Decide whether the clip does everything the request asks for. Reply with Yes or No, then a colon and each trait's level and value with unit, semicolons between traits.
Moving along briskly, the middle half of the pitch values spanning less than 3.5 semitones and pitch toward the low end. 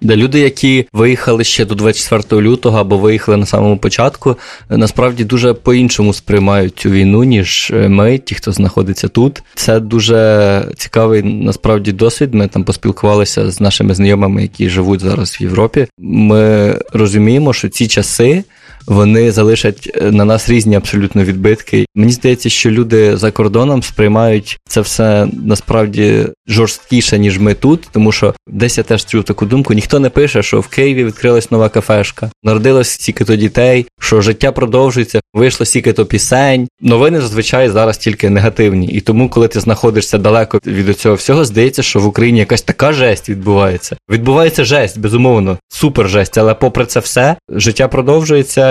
Yes: fast, 160 wpm; average, 2.9 semitones; low, 110 Hz